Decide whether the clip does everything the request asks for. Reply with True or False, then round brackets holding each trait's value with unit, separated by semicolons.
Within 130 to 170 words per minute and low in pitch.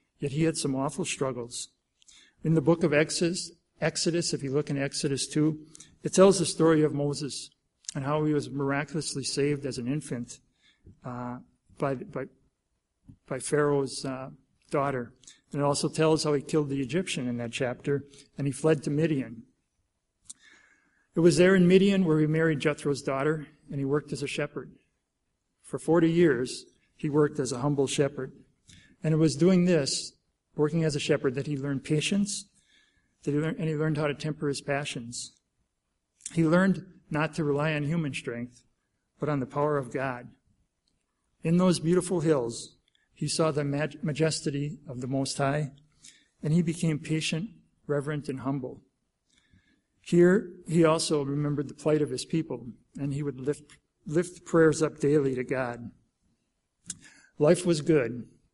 False (165 wpm; 150 Hz)